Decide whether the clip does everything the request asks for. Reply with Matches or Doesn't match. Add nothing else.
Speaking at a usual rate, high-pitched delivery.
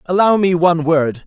Doesn't match